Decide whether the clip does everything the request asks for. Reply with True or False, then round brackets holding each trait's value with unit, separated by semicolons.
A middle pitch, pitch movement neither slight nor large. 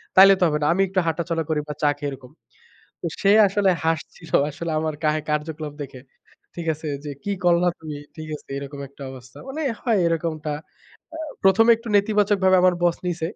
True (165 Hz; 3.9 semitones)